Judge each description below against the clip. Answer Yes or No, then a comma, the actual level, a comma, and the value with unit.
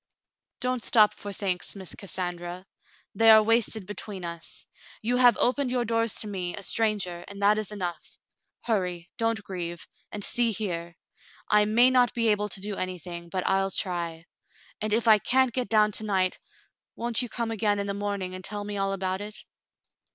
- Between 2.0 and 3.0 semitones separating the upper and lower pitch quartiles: No, average, 3.4 semitones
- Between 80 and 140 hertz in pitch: No, high, 205 Hz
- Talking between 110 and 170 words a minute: No, average, 190 wpm